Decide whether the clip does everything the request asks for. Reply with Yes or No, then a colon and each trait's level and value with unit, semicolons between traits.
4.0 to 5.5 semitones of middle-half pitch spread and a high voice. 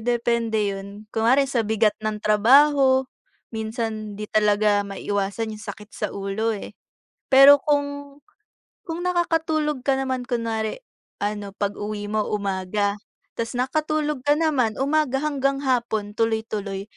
Yes: average, 4.6 semitones; high, 225 Hz